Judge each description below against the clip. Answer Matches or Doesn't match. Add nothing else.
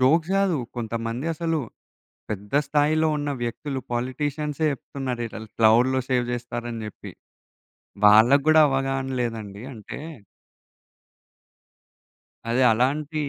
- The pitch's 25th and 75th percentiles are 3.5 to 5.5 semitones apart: Matches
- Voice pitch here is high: Doesn't match